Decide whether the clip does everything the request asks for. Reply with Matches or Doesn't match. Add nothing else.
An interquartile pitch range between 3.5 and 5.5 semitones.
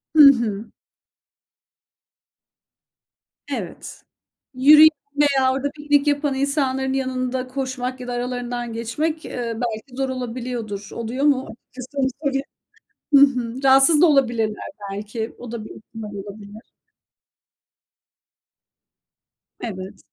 Doesn't match